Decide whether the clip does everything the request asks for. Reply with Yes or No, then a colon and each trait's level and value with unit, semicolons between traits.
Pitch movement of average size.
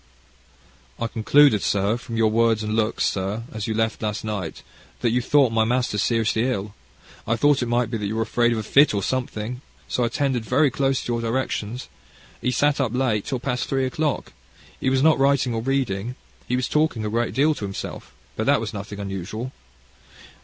Yes: average, 3.3 semitones